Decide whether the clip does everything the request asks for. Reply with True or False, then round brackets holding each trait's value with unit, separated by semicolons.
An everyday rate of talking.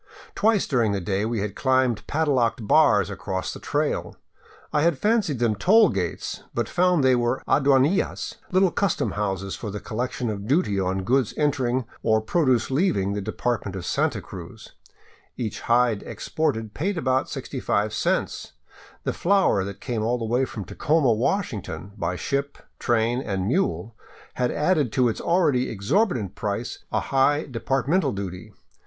True (160 wpm)